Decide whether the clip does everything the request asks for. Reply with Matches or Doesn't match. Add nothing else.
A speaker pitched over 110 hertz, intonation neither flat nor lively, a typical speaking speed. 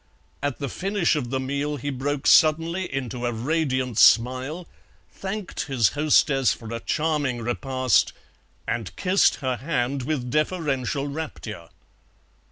Doesn't match